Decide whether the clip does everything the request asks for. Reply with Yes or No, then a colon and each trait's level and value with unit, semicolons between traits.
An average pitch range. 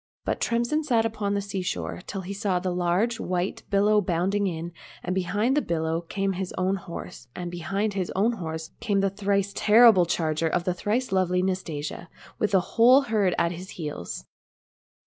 Yes: average, 3.0 semitones